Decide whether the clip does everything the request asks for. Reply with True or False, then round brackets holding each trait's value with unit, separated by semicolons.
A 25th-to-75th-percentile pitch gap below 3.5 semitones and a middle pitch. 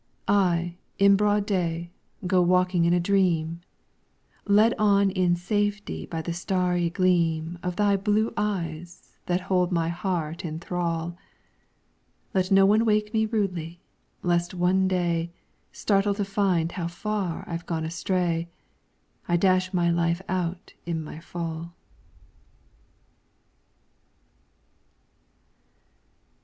True (2.6 semitones; 180 Hz)